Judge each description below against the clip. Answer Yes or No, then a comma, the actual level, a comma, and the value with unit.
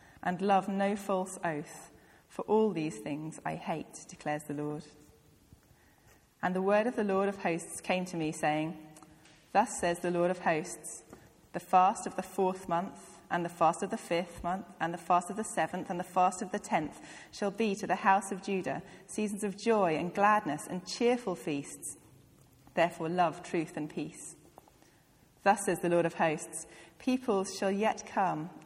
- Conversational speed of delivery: Yes, average, 180 wpm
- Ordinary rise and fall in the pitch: Yes, average, 3.4 semitones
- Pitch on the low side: No, medium, 180 Hz